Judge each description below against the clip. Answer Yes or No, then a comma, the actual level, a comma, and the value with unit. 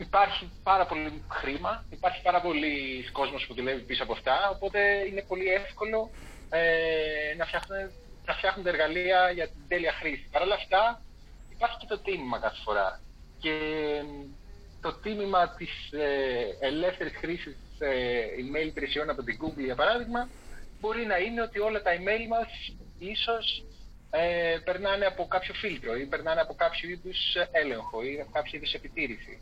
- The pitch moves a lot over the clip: No, average, 4.8 semitones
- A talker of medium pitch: Yes, medium, 175 Hz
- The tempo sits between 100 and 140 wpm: No, average, 160 wpm